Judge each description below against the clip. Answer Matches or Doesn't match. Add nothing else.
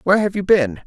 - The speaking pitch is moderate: Matches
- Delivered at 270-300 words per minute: Matches